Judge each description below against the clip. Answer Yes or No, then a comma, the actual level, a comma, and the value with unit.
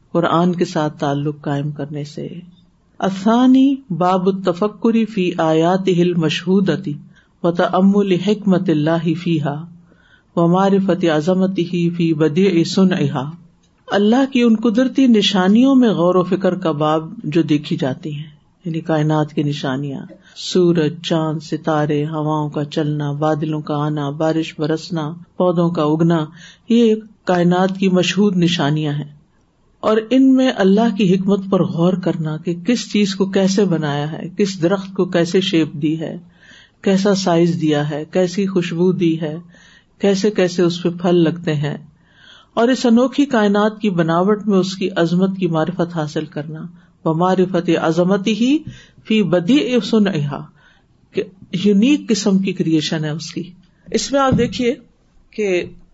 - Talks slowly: No, average, 145 wpm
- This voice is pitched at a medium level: Yes, medium, 175 Hz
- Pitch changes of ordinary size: Yes, average, 3.7 semitones